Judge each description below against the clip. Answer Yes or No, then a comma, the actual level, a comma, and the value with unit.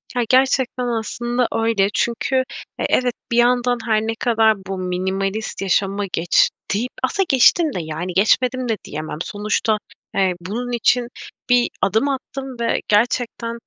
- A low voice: No, high, 230 Hz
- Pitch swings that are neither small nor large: Yes, average, 4.0 semitones